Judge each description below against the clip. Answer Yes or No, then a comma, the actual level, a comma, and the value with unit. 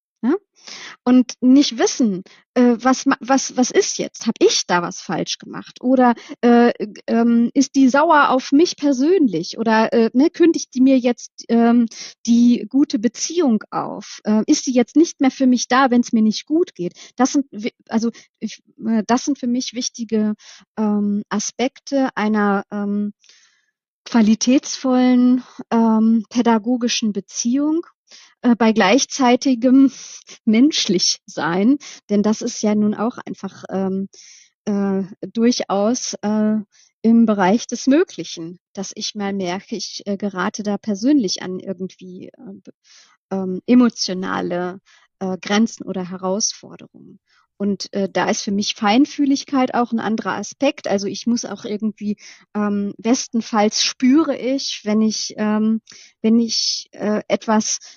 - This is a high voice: Yes, high, 230 Hz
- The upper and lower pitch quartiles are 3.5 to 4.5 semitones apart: Yes, average, 4.1 semitones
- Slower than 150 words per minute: Yes, average, 140 wpm